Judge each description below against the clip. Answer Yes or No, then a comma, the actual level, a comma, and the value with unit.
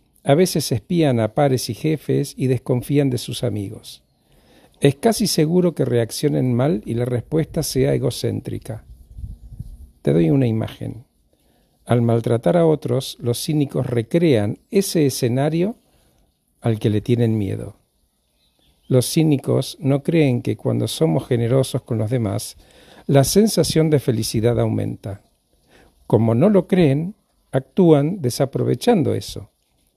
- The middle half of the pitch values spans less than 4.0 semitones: No, average, 4.9 semitones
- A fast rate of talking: No, average, 130 wpm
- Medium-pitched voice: No, low, 130 Hz